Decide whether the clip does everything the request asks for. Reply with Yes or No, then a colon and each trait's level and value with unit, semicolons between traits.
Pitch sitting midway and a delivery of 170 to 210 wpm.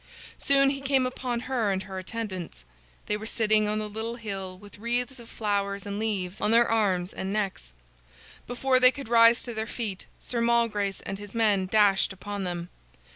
No: high, 215 Hz; average, 185 wpm